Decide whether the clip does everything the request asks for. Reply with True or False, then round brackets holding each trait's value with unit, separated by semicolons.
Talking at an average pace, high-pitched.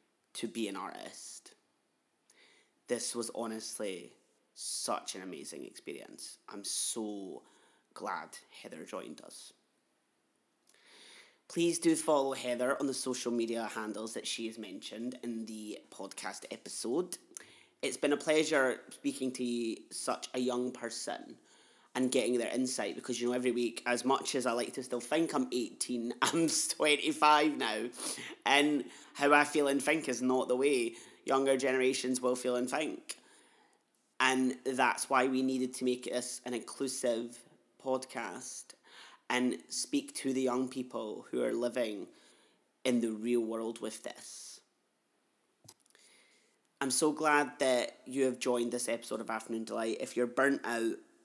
False (145 wpm; 125 Hz)